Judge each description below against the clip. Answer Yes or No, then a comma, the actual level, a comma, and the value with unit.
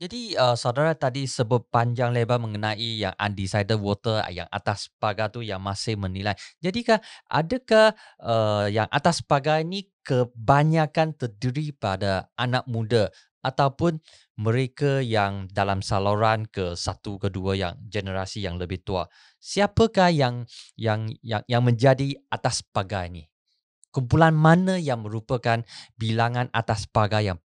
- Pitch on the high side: No, low, 115 Hz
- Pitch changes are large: No, average, 5.0 semitones